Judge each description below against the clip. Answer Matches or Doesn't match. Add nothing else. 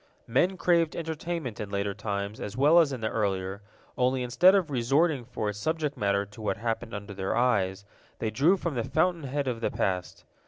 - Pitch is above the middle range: Doesn't match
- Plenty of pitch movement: Matches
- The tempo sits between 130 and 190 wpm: Doesn't match